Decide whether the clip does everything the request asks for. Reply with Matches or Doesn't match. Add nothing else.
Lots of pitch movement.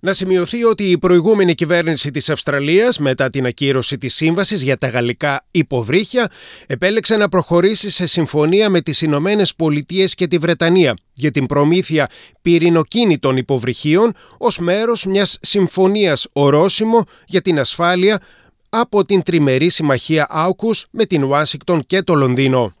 Doesn't match